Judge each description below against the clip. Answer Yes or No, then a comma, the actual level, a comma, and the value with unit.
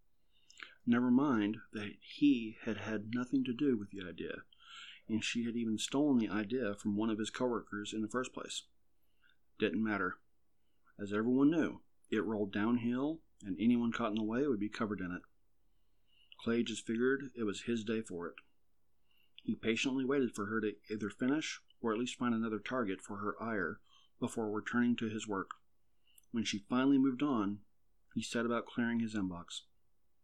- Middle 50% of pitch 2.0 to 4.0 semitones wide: Yes, average, 2.9 semitones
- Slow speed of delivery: No, average, 175 wpm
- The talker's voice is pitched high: No, low, 110 Hz